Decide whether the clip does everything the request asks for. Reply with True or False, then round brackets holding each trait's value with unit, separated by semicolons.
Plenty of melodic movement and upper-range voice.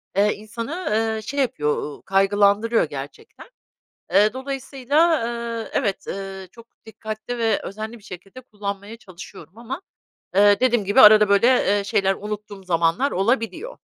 False (3.3 semitones; 210 Hz)